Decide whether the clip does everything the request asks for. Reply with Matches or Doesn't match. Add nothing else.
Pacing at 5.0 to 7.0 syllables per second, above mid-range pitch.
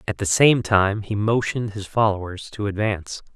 Doesn't match